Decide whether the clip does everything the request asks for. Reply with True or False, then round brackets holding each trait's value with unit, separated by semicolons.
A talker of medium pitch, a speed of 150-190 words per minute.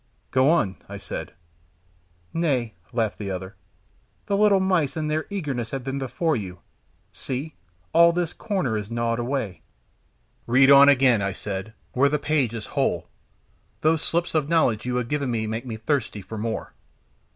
False (130 Hz; 160 wpm)